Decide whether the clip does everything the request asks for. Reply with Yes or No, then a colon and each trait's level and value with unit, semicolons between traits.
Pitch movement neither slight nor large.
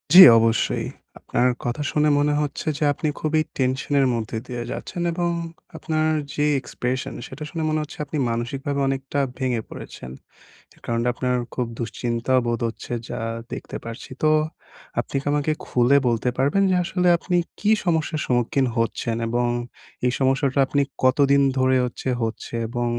Yes: average, 3.7 semitones